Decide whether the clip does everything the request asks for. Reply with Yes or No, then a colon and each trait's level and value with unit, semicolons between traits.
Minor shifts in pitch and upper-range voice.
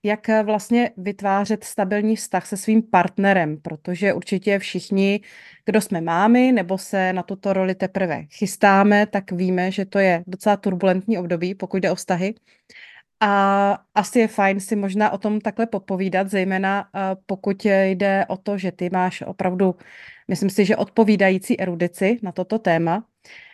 Yes: narrow, 2.0 semitones; high, 195 Hz